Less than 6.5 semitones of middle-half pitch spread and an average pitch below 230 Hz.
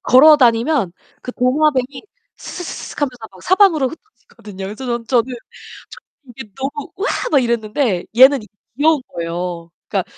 No: average, 5.1 semitones; very high, 255 Hz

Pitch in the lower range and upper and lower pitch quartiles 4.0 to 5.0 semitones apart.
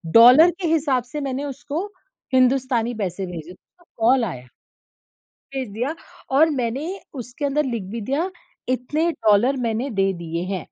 No: very high, 255 Hz; average, 4.4 semitones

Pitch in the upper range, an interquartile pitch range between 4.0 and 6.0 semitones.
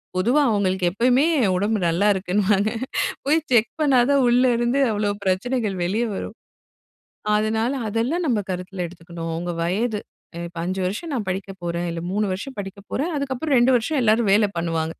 Yes: high, 210 Hz; average, 4.8 semitones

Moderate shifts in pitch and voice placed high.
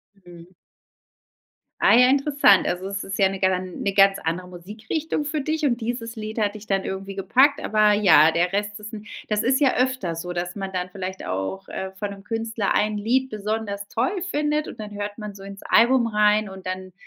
Yes: average, 3.3 semitones; high, 205 Hz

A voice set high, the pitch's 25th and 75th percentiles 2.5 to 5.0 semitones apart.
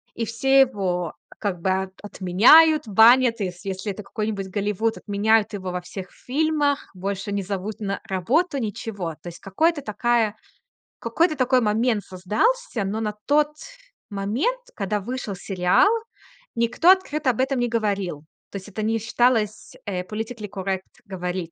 Yes: high, 210 Hz; average, 4.4 semitones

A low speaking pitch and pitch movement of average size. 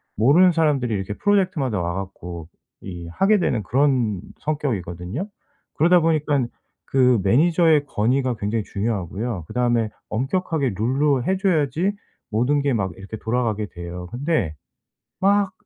No: low, 125 Hz; wide, 7.2 semitones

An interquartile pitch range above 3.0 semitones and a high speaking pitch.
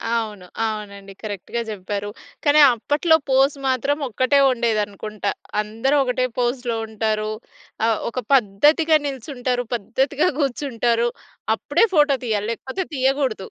Yes: average, 4.3 semitones; high, 240 Hz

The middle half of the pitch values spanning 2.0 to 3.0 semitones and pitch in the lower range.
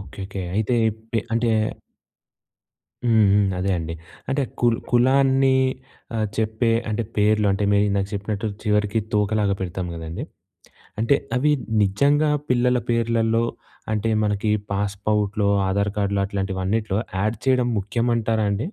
Yes: narrow, 2.6 semitones; low, 105 Hz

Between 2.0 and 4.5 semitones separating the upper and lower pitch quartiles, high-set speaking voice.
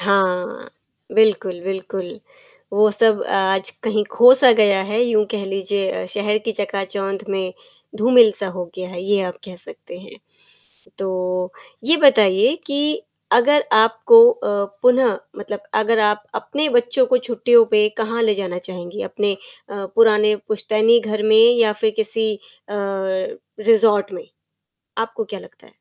Yes: average, 2.9 semitones; high, 210 Hz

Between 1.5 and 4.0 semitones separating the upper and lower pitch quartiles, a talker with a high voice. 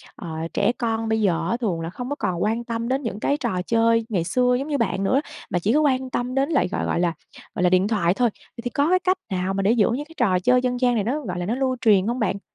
No: average, 5.0 semitones; high, 230 Hz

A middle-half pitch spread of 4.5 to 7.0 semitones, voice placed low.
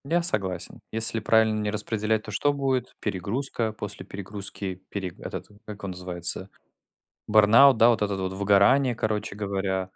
No: narrow, 2.5 semitones; low, 105 Hz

